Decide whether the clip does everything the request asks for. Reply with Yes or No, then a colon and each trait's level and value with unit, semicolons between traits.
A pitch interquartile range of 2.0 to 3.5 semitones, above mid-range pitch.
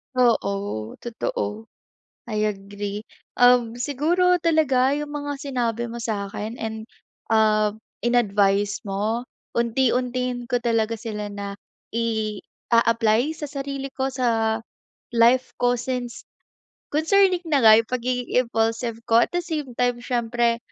Yes: average, 2.8 semitones; high, 235 Hz